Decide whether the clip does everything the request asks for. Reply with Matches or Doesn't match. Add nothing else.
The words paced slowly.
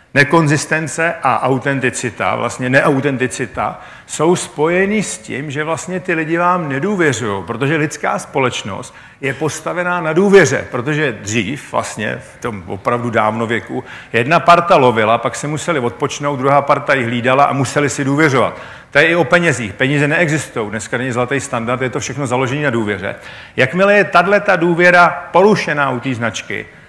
Doesn't match